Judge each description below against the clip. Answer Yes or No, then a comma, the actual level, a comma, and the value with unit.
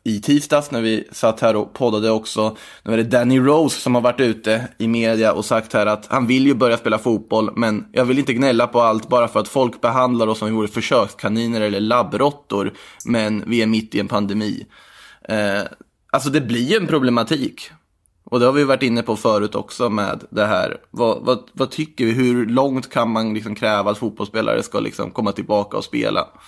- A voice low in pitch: Yes, low, 115 Hz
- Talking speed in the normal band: No, fast, 215 wpm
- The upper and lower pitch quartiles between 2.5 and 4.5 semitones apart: Yes, average, 2.9 semitones